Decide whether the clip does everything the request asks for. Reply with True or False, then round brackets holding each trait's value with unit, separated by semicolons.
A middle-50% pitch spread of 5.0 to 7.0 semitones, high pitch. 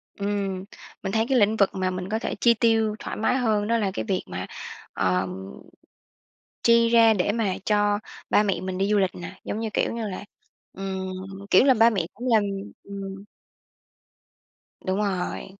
False (2.9 semitones; 205 Hz)